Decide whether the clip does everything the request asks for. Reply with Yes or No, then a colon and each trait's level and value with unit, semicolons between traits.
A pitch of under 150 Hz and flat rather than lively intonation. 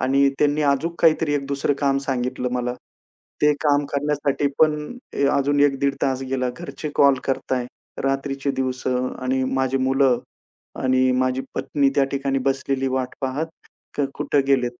Yes: low, 135 Hz; narrow, 1.6 semitones